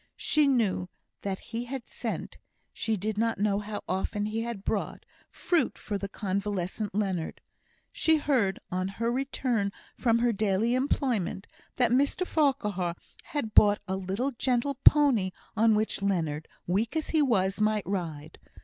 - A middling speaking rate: Yes, average, 150 wpm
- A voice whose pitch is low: No, high, 215 Hz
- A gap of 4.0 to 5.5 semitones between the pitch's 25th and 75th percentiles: Yes, average, 4.3 semitones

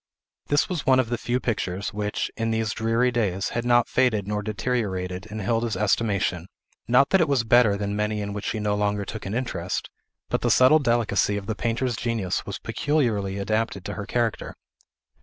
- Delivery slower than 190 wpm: No, average, 195 wpm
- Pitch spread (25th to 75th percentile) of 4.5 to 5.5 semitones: No, average, 3.0 semitones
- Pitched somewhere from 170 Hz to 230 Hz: No, low, 110 Hz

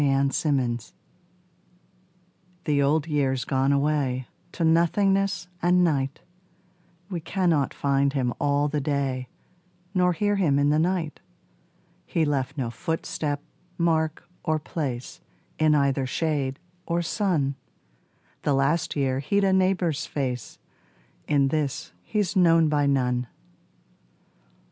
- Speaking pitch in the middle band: Yes, medium, 150 Hz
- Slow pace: Yes, slow, 120 wpm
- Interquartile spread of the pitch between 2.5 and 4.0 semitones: Yes, average, 3.5 semitones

